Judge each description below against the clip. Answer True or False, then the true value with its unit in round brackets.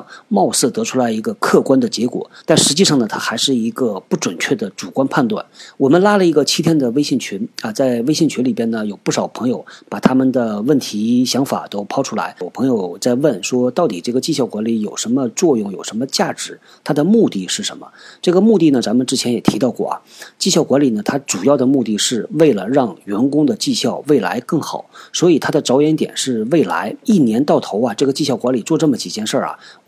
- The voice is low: True (130 Hz)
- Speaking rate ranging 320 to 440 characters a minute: True (330 characters per minute)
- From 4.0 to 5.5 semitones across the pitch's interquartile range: False (6.3 semitones)